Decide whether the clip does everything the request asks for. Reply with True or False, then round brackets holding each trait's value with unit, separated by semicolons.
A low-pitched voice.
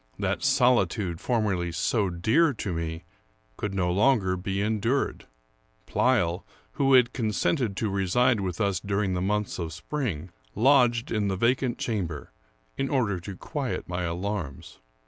True (100 Hz)